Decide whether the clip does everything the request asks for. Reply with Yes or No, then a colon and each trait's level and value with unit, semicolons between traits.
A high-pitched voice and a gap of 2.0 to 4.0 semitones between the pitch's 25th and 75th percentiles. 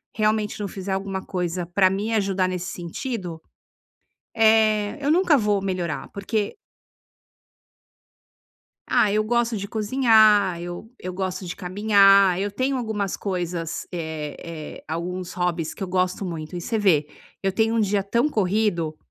Yes: high, 195 Hz; average, 3.2 semitones